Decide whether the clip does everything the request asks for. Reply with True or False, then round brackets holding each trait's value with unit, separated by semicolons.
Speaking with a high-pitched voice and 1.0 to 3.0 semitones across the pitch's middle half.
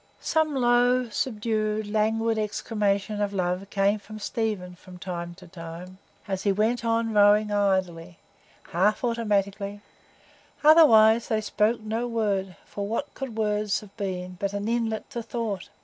True (210 Hz; 2.5 semitones)